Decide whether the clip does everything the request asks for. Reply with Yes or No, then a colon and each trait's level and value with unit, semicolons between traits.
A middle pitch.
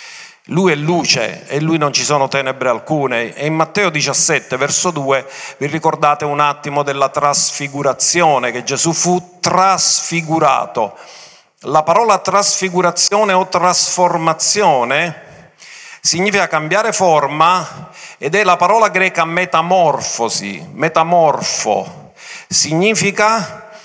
Yes: medium, 170 Hz